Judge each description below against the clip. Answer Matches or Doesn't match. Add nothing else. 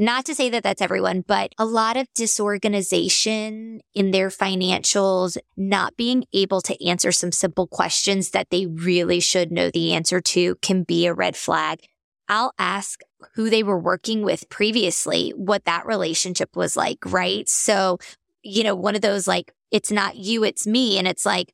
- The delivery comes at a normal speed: Matches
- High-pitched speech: Matches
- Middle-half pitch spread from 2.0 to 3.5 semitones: Matches